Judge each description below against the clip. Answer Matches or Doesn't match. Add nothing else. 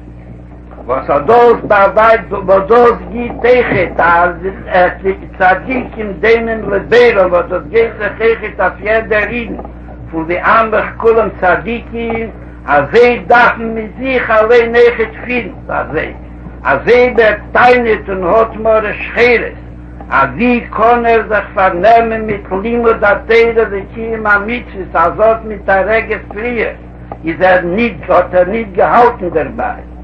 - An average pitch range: Matches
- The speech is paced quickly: Matches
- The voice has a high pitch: Matches